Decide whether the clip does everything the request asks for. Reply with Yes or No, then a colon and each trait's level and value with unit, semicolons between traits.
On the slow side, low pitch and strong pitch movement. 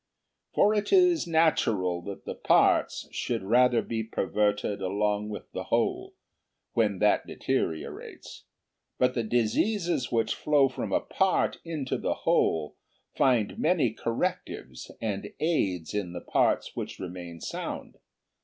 Yes: slow, 130 wpm; low, 115 Hz; wide, 7.4 semitones